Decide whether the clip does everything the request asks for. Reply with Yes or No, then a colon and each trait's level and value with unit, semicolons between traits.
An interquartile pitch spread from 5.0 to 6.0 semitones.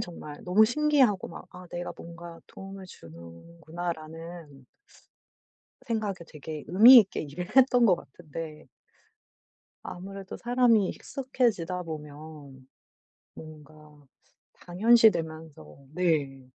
No: average, 4.5 semitones